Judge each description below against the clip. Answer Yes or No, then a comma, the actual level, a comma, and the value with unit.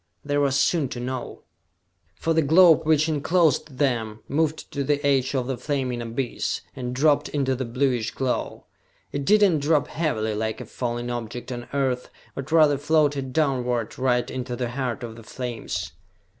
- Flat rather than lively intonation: No, average, 3.2 semitones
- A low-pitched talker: Yes, low, 130 Hz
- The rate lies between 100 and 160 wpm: No, average, 170 wpm